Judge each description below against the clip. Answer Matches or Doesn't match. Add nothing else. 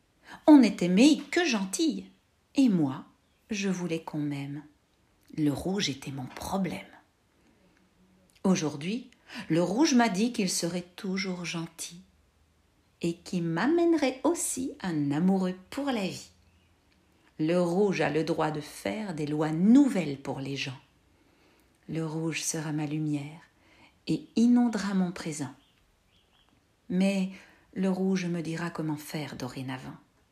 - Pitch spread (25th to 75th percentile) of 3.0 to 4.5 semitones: Doesn't match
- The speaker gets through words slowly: Matches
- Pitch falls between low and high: Matches